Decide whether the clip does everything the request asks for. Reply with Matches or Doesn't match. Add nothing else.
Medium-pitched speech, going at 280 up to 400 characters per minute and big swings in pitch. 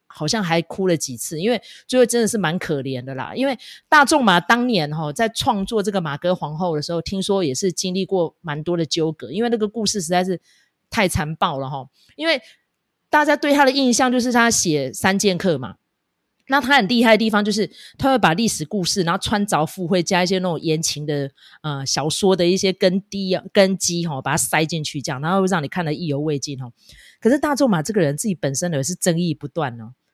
Matches